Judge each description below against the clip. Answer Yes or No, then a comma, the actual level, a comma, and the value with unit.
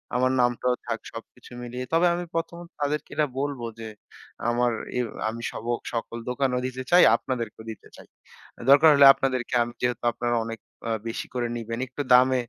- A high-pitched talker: No, low, 125 Hz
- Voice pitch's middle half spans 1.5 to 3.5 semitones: Yes, narrow, 2.5 semitones